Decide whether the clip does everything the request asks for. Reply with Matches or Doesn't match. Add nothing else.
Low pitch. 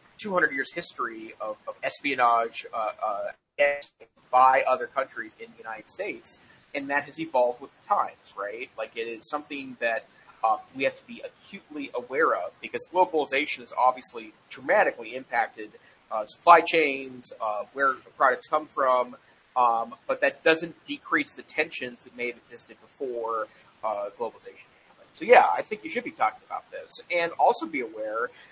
Doesn't match